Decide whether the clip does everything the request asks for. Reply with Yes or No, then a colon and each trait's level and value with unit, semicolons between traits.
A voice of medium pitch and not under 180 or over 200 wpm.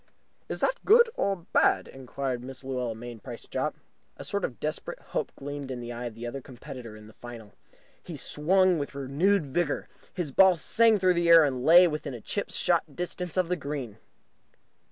Yes: medium, 145 Hz; average, 185 wpm